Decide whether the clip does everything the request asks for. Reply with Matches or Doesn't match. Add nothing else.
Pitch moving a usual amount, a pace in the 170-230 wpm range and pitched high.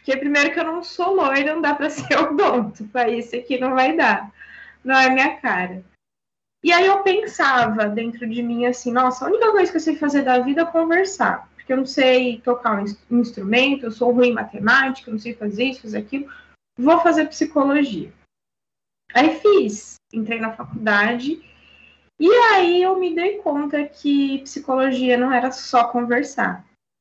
Matches